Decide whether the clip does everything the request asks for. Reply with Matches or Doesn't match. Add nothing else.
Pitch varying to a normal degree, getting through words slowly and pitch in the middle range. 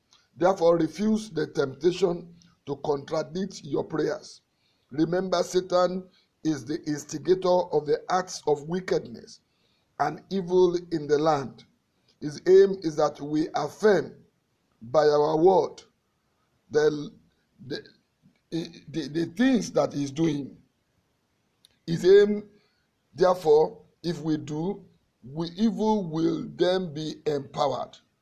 Matches